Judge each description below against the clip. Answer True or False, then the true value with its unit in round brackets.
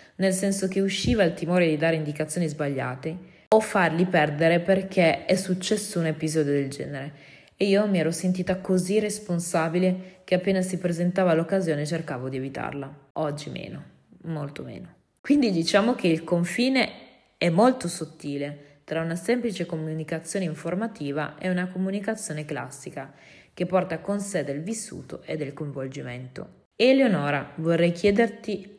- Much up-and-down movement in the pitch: False (4.0 semitones)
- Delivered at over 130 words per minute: True (140 wpm)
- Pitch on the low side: False (175 Hz)